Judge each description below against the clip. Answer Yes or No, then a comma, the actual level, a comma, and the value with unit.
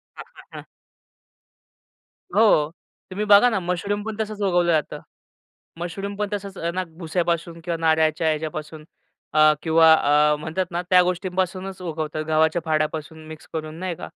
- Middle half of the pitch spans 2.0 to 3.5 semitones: Yes, average, 3.0 semitones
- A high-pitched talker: No, medium, 170 Hz